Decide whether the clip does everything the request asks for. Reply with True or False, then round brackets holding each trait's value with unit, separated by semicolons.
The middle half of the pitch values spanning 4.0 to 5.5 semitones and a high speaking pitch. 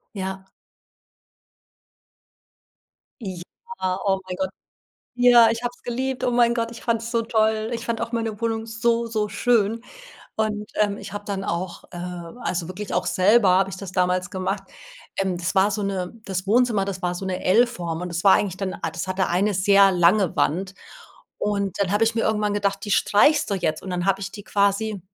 False (3.2 semitones; 200 Hz)